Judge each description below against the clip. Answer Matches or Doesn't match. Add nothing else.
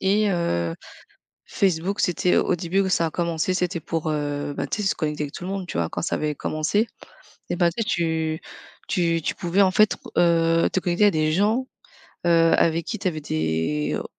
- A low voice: Doesn't match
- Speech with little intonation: Doesn't match